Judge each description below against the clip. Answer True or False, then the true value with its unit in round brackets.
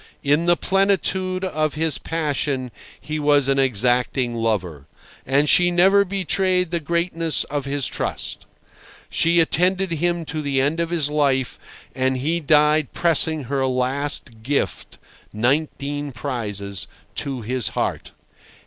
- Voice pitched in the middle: True (145 Hz)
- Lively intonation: False (4.4 semitones)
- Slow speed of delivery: True (130 wpm)